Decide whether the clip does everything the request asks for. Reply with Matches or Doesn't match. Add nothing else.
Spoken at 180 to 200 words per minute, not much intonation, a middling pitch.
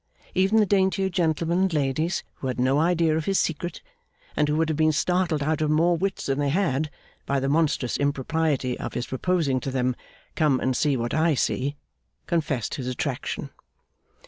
Doesn't match